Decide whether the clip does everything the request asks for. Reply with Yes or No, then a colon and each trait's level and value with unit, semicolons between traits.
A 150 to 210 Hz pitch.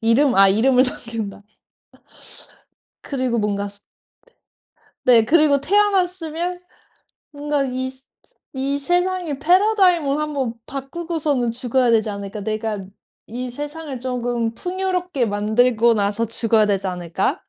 No: very high, 255 Hz